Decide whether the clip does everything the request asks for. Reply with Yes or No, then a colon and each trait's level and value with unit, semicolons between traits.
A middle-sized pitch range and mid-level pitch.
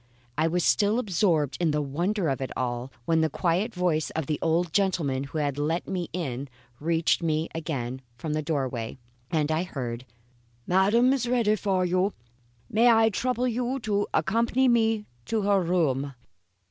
No: wide, 6.0 semitones; medium, 170 Hz